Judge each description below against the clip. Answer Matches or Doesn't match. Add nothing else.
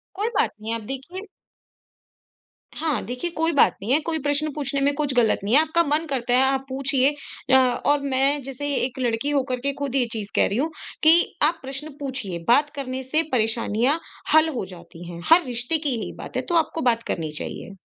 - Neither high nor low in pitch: Doesn't match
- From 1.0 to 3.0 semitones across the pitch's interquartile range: Doesn't match